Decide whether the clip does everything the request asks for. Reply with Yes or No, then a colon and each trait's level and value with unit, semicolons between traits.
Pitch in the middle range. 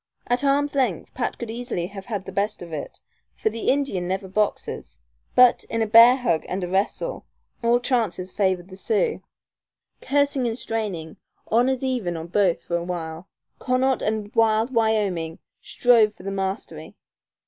No: high, 215 Hz